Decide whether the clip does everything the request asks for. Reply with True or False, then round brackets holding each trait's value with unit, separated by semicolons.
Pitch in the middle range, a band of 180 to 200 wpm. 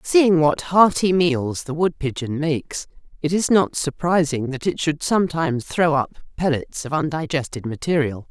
False (155 Hz; 150 wpm)